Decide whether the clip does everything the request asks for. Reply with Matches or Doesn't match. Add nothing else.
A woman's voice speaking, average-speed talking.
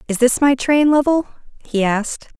Matches